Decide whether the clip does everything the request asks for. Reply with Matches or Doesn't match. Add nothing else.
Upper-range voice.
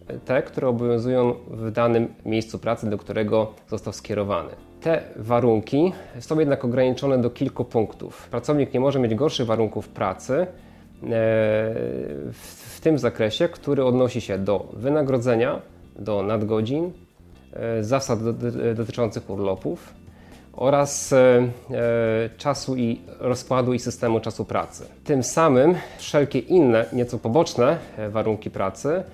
Doesn't match